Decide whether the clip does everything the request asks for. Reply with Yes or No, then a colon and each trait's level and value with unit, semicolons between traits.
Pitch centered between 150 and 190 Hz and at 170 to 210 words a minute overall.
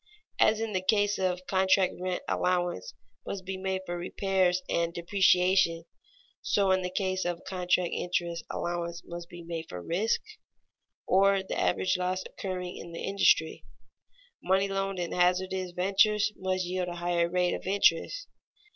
No: medium, 185 Hz; average, 155 wpm